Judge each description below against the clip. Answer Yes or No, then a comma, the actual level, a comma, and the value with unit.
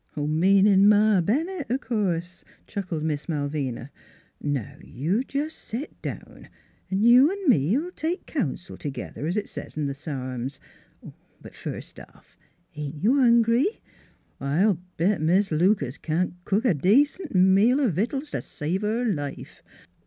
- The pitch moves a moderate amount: No, wide, 7.7 semitones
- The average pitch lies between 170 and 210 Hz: Yes, high, 190 Hz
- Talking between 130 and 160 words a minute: Yes, average, 150 wpm